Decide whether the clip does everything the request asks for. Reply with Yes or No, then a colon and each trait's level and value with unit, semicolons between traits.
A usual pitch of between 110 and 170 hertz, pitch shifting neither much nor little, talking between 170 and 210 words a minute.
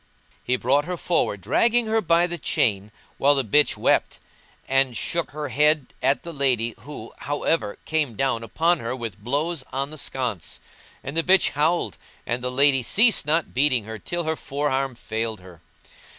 Yes: medium, 140 Hz; average, 5.0 semitones; average, 175 wpm